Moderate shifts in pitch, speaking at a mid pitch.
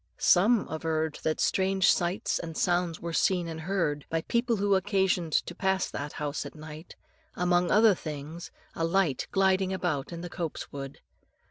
Yes: average, 3.3 semitones; medium, 175 Hz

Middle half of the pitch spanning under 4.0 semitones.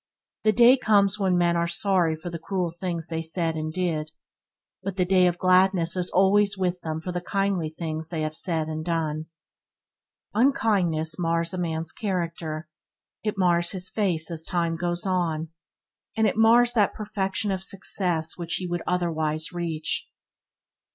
Yes: average, 2.9 semitones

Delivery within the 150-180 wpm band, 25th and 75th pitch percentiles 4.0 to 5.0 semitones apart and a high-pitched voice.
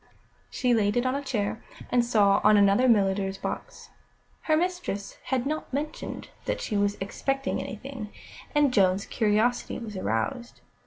Yes: average, 155 wpm; average, 4.5 semitones; high, 225 Hz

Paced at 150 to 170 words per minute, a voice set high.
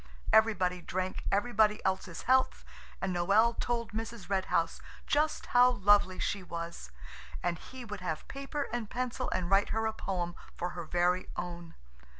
Yes: average, 155 wpm; high, 195 Hz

